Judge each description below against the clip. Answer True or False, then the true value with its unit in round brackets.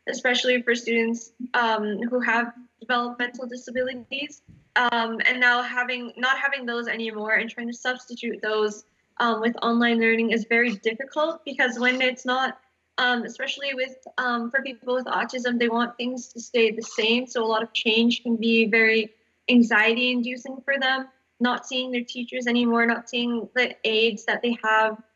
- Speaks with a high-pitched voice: True (240 Hz)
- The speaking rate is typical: True (165 wpm)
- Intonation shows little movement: True (1.8 semitones)